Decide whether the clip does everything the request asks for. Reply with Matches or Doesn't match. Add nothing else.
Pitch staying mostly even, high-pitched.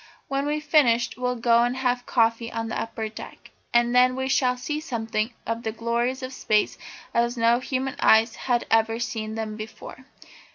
Matches